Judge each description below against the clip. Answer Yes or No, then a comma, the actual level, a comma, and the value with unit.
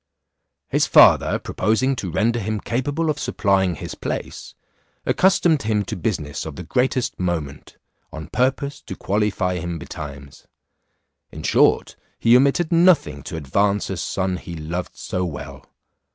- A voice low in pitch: Yes, very low, 95 Hz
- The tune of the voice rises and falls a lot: Yes, wide, 7.2 semitones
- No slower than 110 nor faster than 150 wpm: Yes, average, 140 wpm